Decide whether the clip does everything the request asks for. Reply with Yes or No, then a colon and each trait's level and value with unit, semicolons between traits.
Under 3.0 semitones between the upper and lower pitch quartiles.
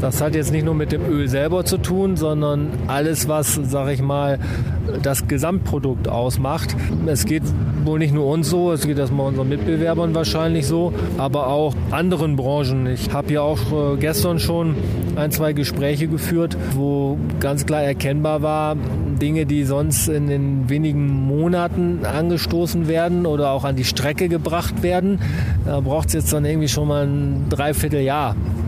Yes: narrow, 2.6 semitones